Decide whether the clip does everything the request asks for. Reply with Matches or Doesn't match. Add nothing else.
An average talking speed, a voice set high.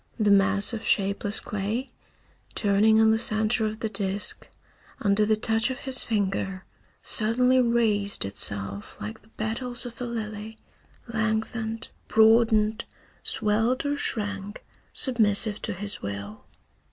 Doesn't match